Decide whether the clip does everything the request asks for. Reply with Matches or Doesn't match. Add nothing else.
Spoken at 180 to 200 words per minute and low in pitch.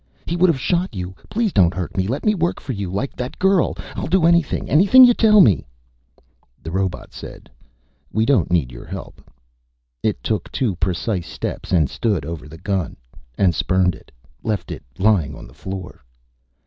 Matches